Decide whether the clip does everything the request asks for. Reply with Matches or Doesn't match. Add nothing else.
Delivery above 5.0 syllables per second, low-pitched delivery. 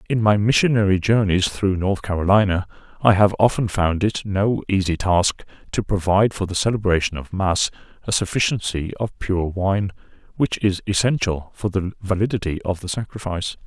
Matches